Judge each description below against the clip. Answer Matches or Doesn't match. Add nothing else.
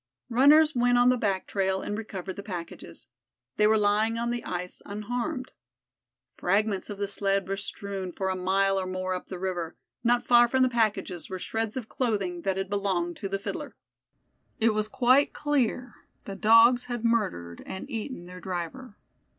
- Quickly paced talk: Doesn't match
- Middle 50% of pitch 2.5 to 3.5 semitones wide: Doesn't match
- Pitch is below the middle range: Doesn't match